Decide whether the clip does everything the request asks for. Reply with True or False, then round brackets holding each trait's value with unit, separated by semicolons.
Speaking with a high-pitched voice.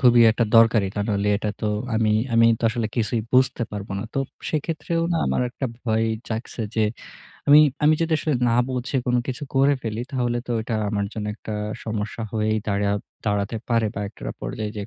False (115 Hz)